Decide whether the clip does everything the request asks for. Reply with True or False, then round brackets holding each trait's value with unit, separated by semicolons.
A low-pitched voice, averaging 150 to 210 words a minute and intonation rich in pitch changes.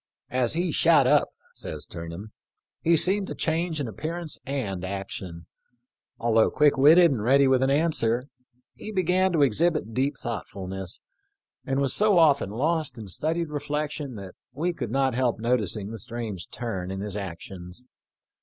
True (130 Hz; 160 wpm; 7.0 semitones)